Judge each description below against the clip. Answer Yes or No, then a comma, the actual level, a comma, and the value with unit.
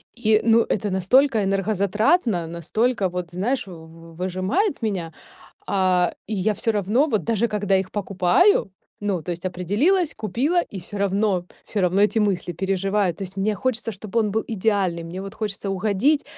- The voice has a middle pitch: No, high, 200 Hz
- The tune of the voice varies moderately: Yes, average, 3.3 semitones